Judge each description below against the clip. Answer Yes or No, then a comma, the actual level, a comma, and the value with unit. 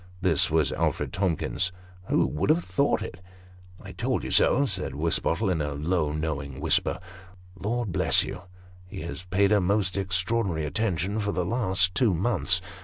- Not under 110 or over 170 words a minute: No, average, 180 wpm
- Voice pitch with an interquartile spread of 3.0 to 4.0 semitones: Yes, average, 3.6 semitones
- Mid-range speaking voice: No, very low, 90 Hz